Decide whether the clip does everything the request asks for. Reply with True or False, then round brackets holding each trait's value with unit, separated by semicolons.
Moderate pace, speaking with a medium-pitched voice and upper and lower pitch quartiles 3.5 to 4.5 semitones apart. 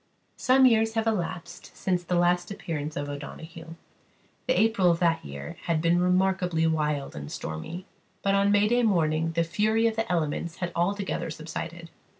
True (160 wpm; 175 Hz; 3.8 semitones)